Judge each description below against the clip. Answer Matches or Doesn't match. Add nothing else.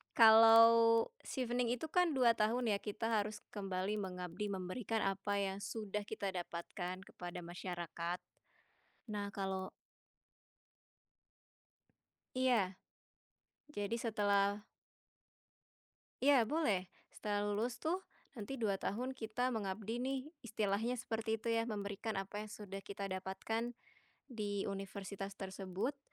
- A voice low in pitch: Doesn't match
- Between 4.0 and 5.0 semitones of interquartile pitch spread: Doesn't match